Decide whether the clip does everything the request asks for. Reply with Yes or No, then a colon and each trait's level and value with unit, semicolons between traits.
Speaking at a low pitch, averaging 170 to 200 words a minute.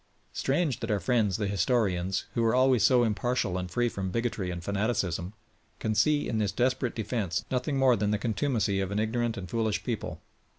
Yes: low, 110 Hz; average, 195 wpm